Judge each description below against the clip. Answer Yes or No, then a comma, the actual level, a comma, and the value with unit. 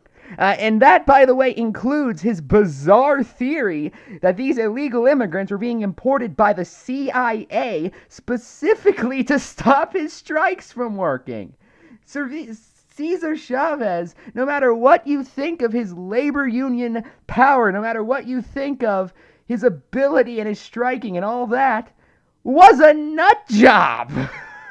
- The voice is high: Yes, very high, 250 Hz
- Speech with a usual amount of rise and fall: Yes, average, 4.3 semitones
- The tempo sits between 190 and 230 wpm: No, average, 140 wpm